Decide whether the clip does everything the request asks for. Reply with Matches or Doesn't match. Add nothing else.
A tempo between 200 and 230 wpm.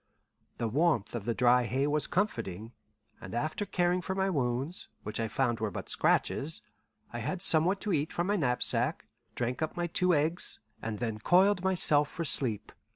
Doesn't match